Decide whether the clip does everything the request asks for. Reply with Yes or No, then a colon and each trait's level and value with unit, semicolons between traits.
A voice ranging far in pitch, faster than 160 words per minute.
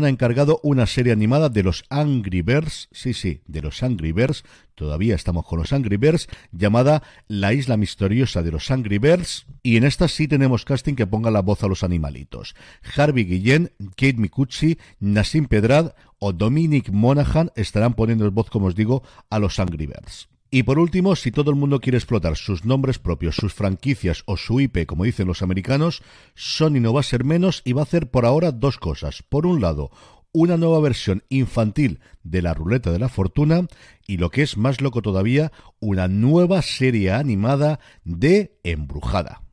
Yes: wide, 6.4 semitones; average, 185 wpm